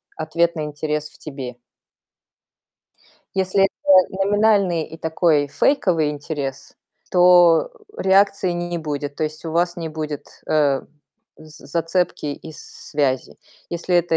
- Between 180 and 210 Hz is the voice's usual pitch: No, medium, 165 Hz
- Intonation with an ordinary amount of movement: Yes, average, 3.0 semitones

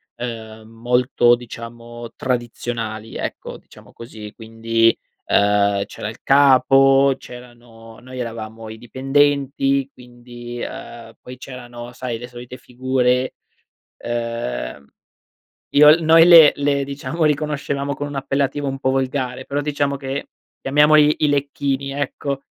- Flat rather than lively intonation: No, average, 3.0 semitones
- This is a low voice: Yes, low, 125 Hz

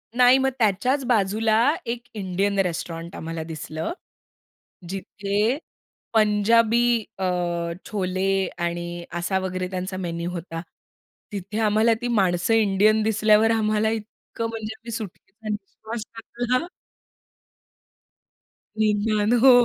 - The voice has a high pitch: Yes, high, 210 Hz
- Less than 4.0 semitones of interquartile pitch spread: Yes, average, 3.3 semitones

